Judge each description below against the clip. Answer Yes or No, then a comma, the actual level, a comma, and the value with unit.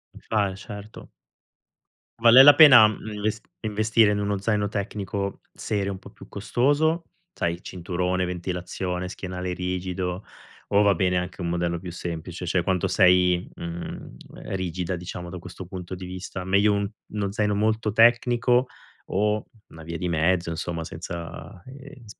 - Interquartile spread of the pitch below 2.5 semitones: No, average, 2.9 semitones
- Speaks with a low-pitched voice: Yes, very low, 95 Hz